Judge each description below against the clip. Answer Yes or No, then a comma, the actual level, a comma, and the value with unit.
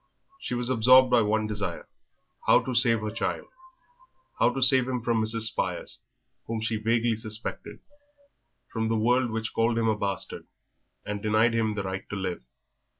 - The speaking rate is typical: Yes, average, 175 wpm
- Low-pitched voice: Yes, low, 115 Hz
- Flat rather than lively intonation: Yes, narrow, 1.9 semitones